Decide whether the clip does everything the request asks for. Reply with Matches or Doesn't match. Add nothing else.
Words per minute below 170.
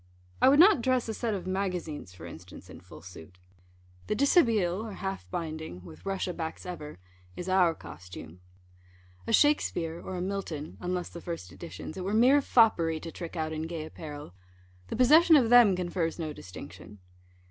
Doesn't match